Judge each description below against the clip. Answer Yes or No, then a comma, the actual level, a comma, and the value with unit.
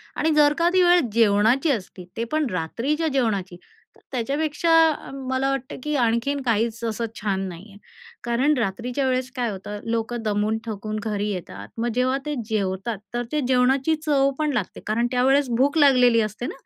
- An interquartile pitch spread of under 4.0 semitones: No, average, 4.3 semitones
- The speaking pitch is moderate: No, high, 240 Hz